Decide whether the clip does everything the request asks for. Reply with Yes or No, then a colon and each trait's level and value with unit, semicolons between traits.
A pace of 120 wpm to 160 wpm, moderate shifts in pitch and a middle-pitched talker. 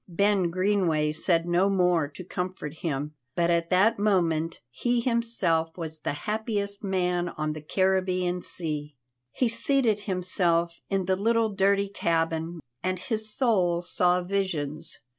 Yes: average, 140 wpm; average, 3.3 semitones; medium, 180 Hz